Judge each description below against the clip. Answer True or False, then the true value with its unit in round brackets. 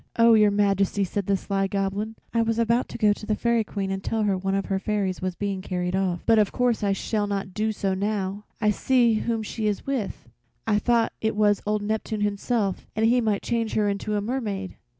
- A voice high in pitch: True (210 Hz)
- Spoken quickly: True (230 wpm)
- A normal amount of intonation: False (2.2 semitones)